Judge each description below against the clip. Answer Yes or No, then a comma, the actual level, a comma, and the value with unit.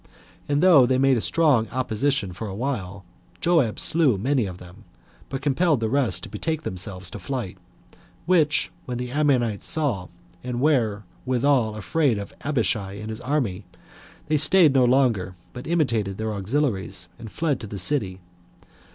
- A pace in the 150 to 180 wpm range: Yes, average, 160 wpm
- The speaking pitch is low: Yes, low, 125 Hz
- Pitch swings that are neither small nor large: No, wide, 5.9 semitones